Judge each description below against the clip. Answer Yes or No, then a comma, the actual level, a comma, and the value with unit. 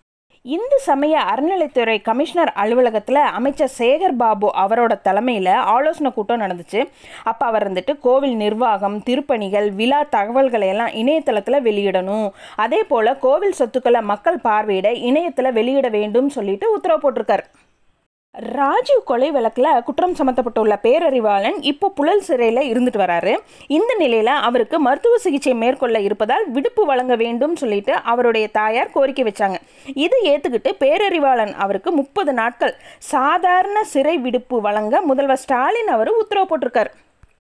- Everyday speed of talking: Yes, average, 120 wpm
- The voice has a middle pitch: No, very high, 255 Hz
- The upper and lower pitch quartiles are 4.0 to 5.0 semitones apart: No, wide, 5.4 semitones